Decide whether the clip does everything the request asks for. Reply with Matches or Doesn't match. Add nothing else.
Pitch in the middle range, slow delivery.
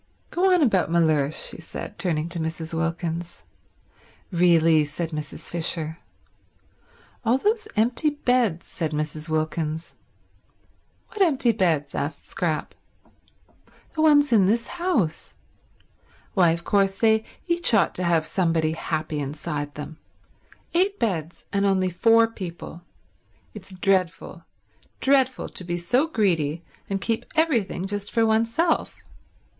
Matches